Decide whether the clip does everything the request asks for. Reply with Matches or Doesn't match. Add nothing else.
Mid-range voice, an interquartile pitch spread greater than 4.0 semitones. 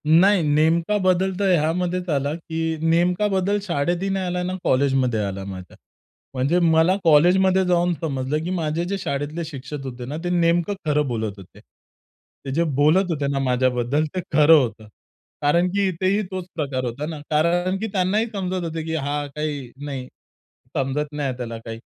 Matches